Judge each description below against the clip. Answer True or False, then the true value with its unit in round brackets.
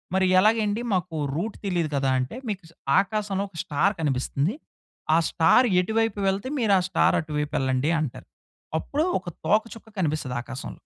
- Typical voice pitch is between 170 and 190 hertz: True (185 Hz)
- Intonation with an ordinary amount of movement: False (6.0 semitones)